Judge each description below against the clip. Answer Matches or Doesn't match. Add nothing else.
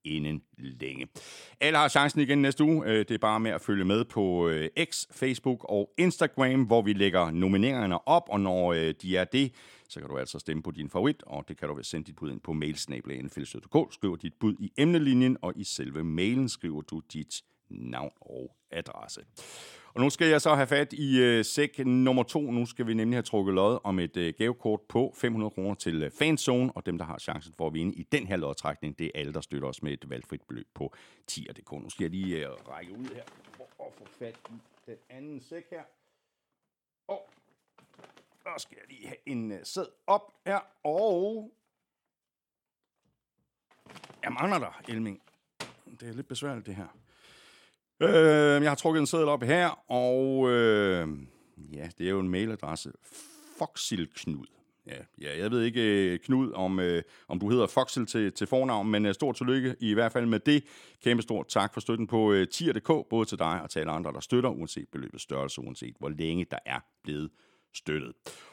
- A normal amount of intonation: Doesn't match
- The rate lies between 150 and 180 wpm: Doesn't match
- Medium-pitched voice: Doesn't match